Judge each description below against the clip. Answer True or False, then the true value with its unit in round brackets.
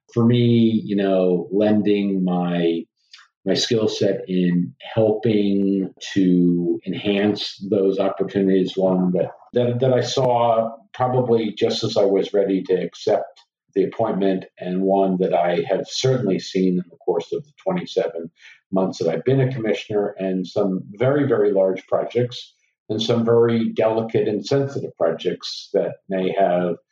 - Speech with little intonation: False (3.7 semitones)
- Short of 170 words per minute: True (145 wpm)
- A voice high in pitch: False (100 Hz)